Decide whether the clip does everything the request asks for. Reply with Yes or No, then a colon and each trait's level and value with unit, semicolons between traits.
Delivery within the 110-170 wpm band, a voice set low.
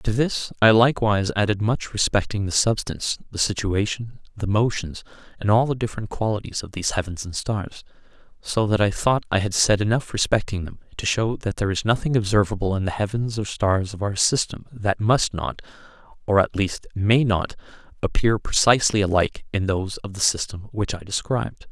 No: average, 185 wpm; low, 105 Hz